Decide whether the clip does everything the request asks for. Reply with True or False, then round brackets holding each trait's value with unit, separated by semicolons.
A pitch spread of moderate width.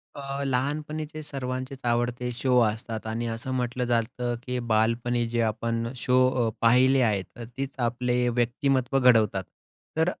False (1.9 semitones)